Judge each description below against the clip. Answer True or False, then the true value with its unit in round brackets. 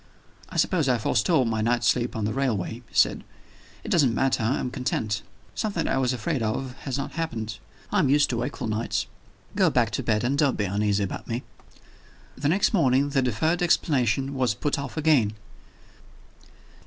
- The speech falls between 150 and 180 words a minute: False (190 wpm)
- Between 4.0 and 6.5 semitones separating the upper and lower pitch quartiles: True (4.3 semitones)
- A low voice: True (125 Hz)